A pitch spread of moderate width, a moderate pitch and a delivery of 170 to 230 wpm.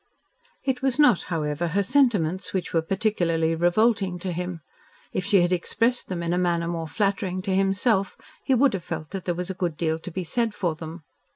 Yes: average, 3.2 semitones; medium, 180 Hz; fast, 205 wpm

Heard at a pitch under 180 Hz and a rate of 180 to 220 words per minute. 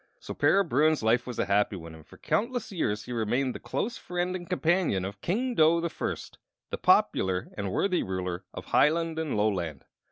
Yes: low, 135 Hz; average, 195 wpm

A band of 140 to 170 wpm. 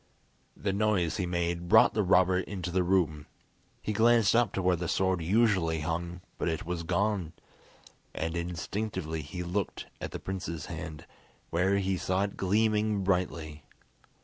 Yes: average, 155 wpm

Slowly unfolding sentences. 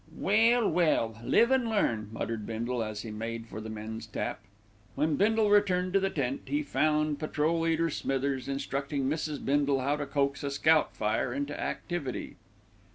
No: average, 170 wpm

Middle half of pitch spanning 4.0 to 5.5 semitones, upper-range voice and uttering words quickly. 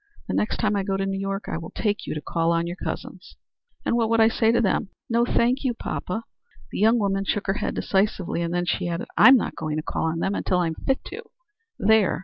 Yes: average, 4.4 semitones; high, 195 Hz; fast, 250 wpm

